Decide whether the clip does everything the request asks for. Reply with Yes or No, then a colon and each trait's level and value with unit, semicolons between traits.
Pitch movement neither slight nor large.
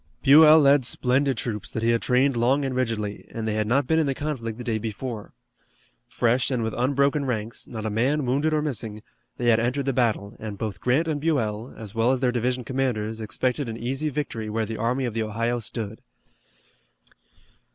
Yes: average, 3.4 semitones